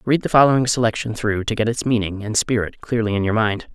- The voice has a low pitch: Yes, low, 110 Hz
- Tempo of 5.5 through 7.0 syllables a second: Yes, 6.1 syllables/s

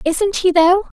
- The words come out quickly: No, average, 185 wpm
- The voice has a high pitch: Yes, very high, 360 Hz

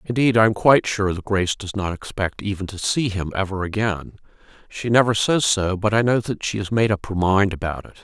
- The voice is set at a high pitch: No, low, 100 Hz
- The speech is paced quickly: Yes, fast, 240 wpm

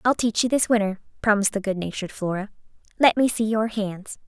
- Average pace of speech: Yes, average, 195 wpm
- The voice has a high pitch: Yes, high, 210 Hz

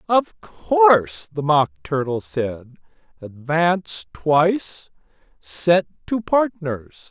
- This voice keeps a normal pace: No, slow, 95 wpm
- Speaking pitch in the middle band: Yes, medium, 160 Hz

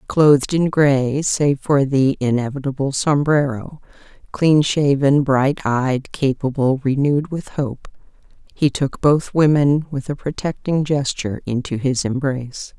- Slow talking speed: Yes, slow, 125 wpm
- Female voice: Yes, female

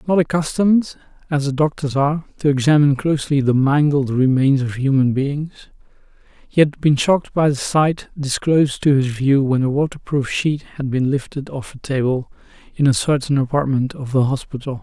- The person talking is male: Yes, male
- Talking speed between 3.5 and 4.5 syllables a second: No, 5.3 syllables/s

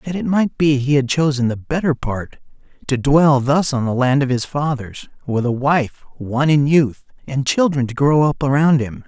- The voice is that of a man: Yes, male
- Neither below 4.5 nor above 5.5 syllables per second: Yes, 4.7 syllables/s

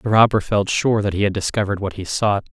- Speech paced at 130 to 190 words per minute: No, fast, 260 wpm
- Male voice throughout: Yes, male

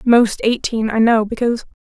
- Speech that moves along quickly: No, average, 160 wpm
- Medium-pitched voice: No, high, 225 Hz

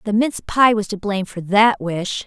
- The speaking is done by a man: No, female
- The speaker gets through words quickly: Yes, fast, 240 wpm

